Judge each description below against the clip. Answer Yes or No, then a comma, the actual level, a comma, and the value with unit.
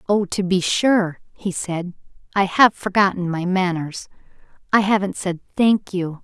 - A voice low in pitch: No, high, 190 Hz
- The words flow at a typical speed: Yes, average, 155 wpm